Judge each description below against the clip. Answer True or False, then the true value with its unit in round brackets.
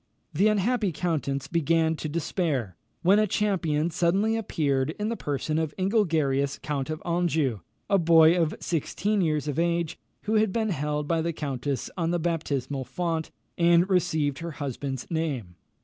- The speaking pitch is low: False (165 Hz)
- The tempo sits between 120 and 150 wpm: False (160 wpm)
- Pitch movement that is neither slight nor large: True (3.5 semitones)